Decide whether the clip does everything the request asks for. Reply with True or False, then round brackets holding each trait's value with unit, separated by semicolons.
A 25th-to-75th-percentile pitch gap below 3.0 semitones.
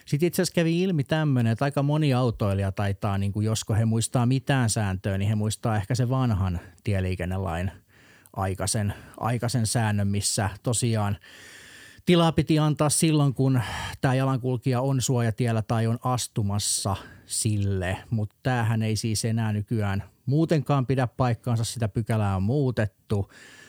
False (4.1 semitones)